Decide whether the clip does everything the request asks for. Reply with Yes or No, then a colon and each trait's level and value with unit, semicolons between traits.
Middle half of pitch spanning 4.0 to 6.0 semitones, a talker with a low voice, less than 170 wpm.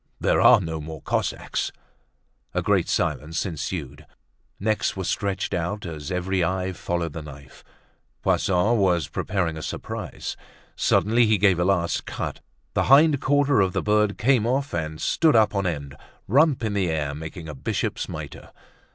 Yes: average, 4.9 semitones; very low, 95 Hz; average, 160 wpm